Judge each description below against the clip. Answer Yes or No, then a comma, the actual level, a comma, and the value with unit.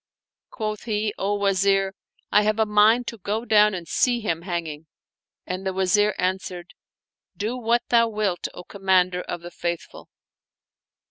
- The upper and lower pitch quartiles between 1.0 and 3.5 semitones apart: Yes, average, 2.8 semitones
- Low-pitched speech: No, high, 200 Hz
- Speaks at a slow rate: No, average, 165 wpm